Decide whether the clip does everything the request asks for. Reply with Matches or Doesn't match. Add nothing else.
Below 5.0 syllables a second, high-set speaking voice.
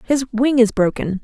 Matches